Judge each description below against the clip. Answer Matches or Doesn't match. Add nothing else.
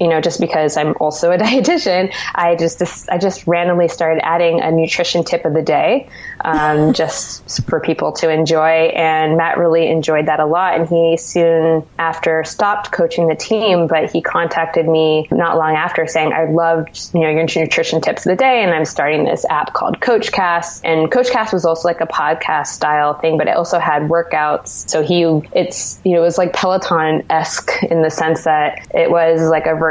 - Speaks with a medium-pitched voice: Matches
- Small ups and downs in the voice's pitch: Matches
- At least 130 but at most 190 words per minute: Doesn't match